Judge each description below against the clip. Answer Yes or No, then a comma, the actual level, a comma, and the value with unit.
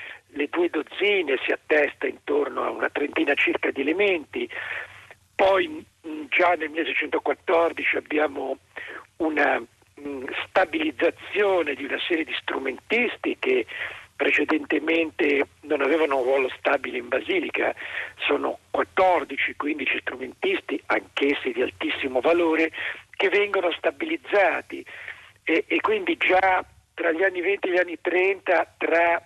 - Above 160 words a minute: No, average, 120 wpm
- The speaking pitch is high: Yes, high, 195 Hz